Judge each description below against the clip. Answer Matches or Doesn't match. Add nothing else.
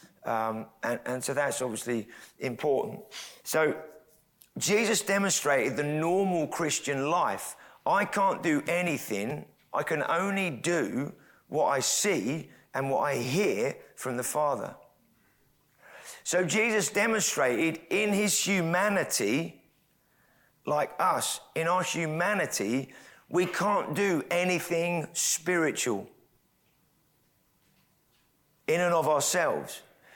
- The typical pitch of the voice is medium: Matches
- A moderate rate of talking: Doesn't match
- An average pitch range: Matches